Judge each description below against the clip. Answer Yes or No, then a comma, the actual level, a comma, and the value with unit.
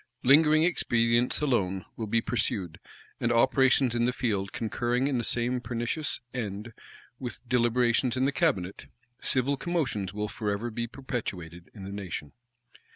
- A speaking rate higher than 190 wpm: No, average, 145 wpm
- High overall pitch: No, low, 120 Hz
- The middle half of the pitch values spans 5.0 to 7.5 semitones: No, average, 3.5 semitones